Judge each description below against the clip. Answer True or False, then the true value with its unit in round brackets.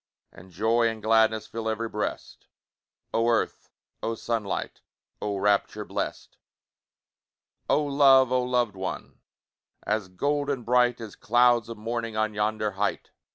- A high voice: False (115 Hz)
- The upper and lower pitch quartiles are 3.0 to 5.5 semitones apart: False (2.4 semitones)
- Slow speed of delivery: True (130 wpm)